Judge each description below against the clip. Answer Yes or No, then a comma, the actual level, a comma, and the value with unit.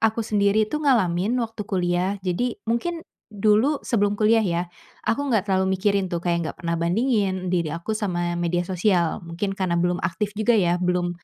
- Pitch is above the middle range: Yes, high, 195 Hz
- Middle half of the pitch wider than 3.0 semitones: Yes, average, 3.7 semitones